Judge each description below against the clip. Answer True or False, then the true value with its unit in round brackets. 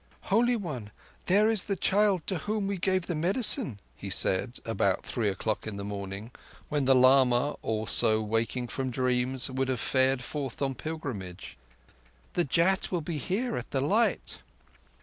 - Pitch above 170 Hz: False (135 Hz)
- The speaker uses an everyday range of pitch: False (8.2 semitones)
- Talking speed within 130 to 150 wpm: False (165 wpm)